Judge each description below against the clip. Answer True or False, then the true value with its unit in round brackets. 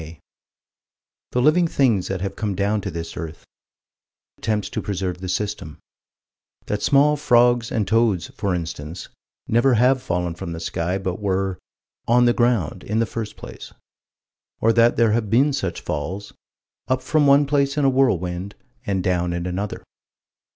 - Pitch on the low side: True (105 Hz)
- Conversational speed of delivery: True (165 wpm)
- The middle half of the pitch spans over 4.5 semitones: True (5.2 semitones)